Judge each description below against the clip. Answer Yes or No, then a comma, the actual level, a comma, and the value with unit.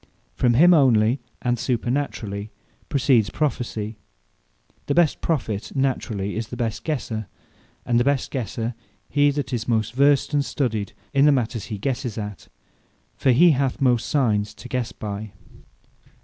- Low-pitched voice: Yes, low, 120 Hz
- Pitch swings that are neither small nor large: Yes, average, 4.1 semitones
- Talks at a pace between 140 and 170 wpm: Yes, average, 150 wpm